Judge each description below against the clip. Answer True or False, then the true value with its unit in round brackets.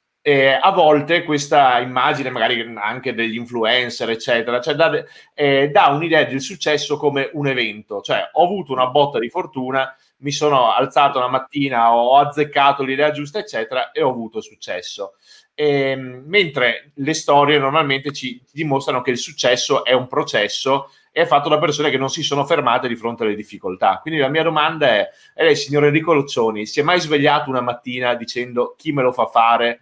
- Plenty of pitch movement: False (3.4 semitones)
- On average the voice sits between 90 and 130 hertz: False (140 Hz)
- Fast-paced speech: True (180 wpm)